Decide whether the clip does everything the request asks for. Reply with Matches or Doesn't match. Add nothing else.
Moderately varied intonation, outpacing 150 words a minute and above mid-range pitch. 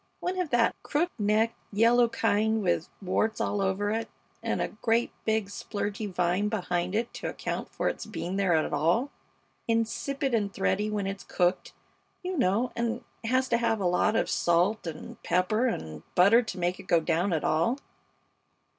Matches